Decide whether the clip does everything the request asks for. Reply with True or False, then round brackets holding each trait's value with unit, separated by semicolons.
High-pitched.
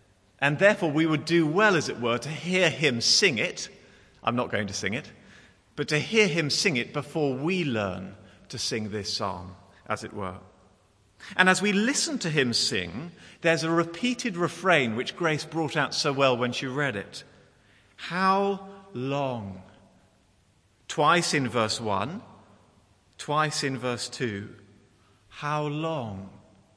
False (130 Hz)